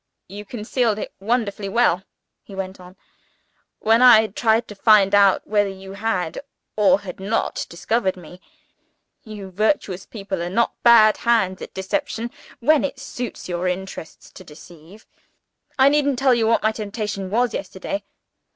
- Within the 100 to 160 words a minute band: Yes, average, 150 wpm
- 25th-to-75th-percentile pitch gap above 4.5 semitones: No, average, 3.6 semitones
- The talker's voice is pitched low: No, high, 210 Hz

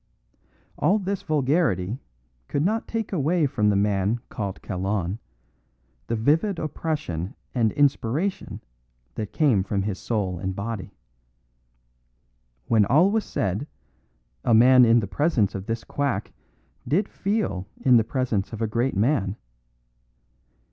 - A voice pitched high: No, low, 115 Hz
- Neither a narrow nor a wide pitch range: No, wide, 7.2 semitones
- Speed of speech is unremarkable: No, slow, 130 wpm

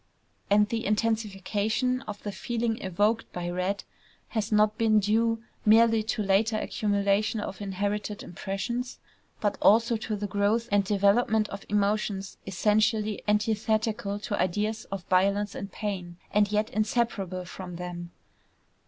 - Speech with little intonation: Yes, narrow, 1.9 semitones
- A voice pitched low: No, high, 210 Hz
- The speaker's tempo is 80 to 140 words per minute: Yes, slow, 135 wpm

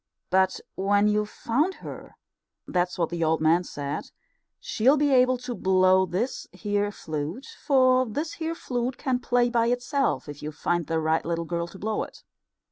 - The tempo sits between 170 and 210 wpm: Yes, average, 175 wpm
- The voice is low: No, high, 205 Hz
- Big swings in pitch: Yes, wide, 6.7 semitones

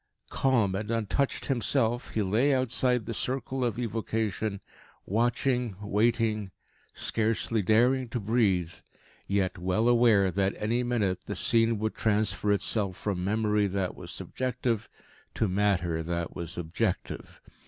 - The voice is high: No, low, 110 Hz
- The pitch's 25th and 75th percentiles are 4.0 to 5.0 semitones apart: No, average, 3.3 semitones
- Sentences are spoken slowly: Yes, slow, 130 wpm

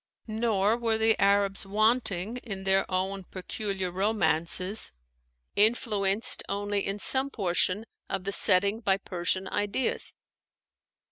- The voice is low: No, high, 200 Hz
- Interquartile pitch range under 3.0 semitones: Yes, narrow, 2.4 semitones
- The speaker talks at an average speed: No, slow, 115 wpm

